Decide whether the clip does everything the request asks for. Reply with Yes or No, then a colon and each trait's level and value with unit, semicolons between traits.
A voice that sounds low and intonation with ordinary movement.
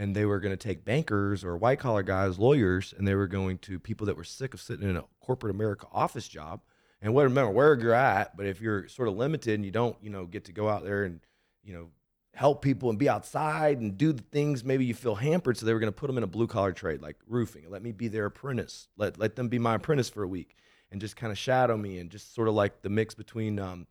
Yes: low, 110 Hz; average, 3.6 semitones